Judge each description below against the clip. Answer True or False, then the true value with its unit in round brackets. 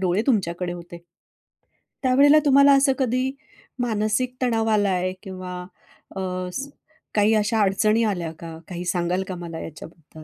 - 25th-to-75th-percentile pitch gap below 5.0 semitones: False (5.5 semitones)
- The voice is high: True (200 Hz)